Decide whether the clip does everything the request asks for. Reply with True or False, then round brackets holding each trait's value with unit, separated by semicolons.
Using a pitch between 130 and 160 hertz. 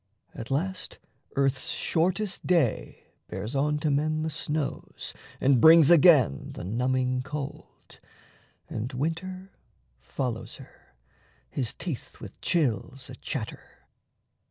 True (140 Hz)